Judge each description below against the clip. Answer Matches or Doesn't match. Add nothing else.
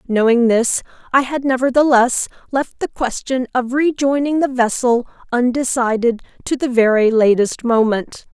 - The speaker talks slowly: Matches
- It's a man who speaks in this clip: Doesn't match